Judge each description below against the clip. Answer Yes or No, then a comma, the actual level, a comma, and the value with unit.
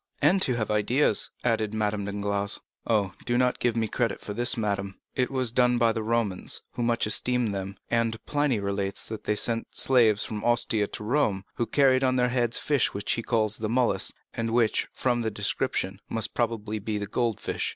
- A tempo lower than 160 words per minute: No, average, 195 wpm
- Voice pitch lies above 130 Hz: No, low, 115 Hz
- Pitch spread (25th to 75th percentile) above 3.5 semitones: No, average, 2.7 semitones